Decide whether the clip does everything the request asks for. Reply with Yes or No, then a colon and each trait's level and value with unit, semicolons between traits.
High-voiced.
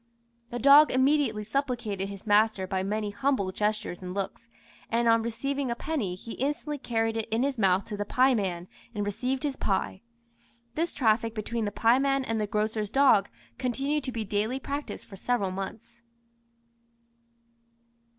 Yes: high, 225 Hz